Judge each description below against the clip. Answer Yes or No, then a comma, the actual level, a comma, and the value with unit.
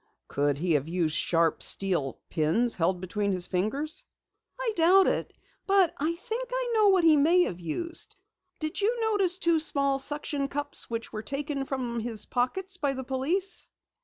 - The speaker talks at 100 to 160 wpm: No, average, 170 wpm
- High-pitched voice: Yes, very high, 280 Hz